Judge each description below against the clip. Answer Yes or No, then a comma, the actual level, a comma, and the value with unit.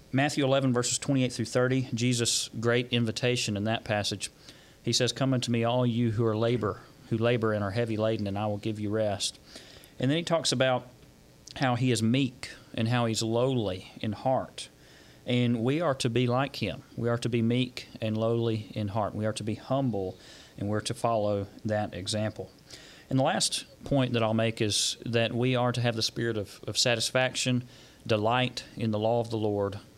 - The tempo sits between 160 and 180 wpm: No, average, 200 wpm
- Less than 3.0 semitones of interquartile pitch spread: Yes, narrow, 2.6 semitones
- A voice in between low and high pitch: No, low, 115 Hz